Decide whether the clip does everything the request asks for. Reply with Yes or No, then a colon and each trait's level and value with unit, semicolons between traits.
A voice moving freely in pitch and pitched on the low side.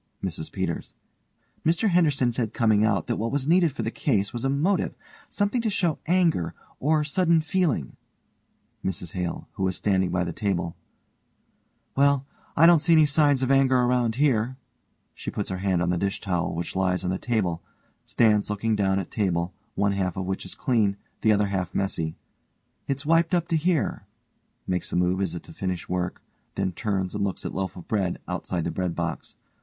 Yes: wide, 7.5 semitones; low, 105 Hz